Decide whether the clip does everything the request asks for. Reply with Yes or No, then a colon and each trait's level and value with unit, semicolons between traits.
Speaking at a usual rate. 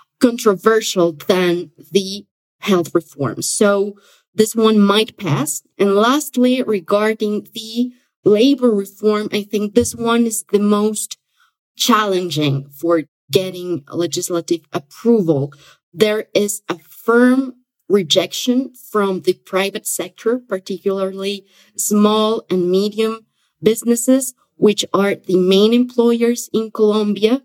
No: slow, 105 wpm